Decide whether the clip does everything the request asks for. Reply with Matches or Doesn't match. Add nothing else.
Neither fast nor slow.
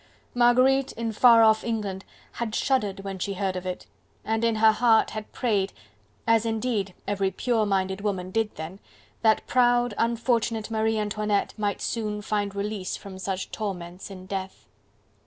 Matches